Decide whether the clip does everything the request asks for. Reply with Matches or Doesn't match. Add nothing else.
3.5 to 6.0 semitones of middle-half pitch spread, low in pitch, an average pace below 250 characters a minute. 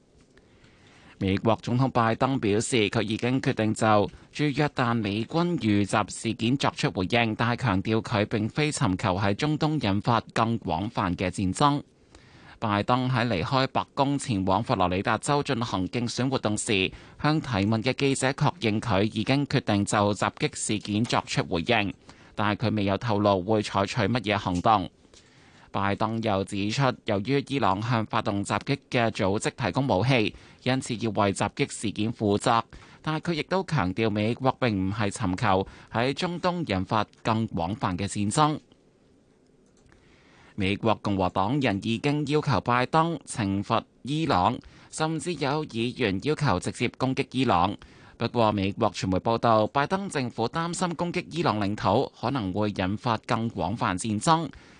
Matches